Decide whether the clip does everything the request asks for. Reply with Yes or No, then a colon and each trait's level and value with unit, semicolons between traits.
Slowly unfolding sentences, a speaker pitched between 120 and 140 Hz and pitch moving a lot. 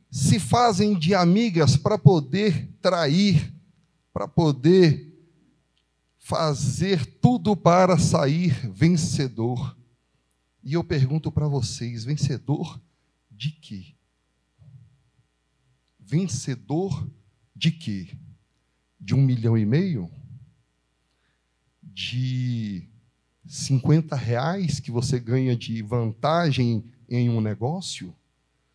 Yes: slow, 85 wpm; low, 135 Hz; wide, 5.9 semitones